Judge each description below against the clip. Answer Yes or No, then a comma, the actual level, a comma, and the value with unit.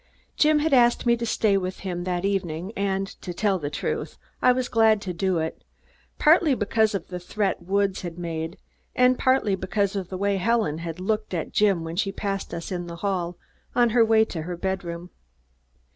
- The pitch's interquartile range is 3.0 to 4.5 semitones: Yes, average, 3.9 semitones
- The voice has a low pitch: No, high, 195 Hz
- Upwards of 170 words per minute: Yes, average, 195 wpm